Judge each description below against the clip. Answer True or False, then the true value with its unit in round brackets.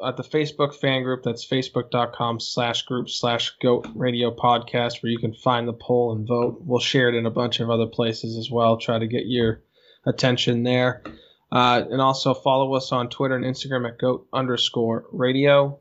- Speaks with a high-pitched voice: False (125 Hz)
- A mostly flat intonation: True (1.6 semitones)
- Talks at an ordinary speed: True (195 wpm)